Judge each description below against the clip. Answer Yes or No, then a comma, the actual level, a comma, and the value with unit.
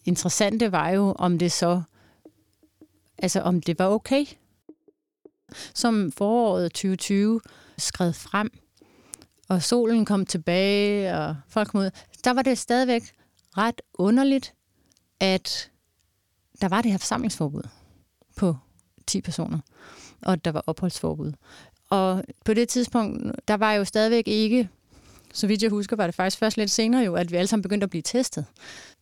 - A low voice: No, high, 200 Hz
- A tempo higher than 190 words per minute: No, average, 150 wpm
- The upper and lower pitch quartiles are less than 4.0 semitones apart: No, average, 4.6 semitones